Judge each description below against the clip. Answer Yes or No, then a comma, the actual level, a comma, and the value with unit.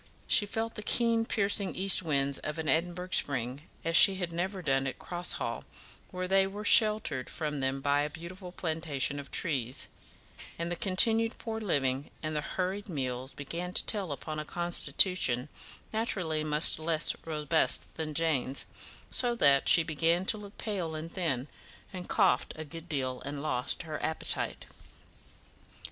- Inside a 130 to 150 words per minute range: No, average, 160 wpm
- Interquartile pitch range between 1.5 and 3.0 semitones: No, average, 4.7 semitones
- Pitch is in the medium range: Yes, medium, 165 Hz